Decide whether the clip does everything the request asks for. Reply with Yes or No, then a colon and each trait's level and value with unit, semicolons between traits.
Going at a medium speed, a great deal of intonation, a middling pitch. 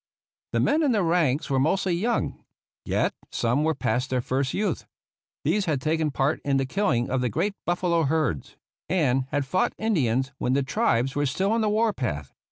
Yes: average, 190 wpm; wide, 6.3 semitones; medium, 150 Hz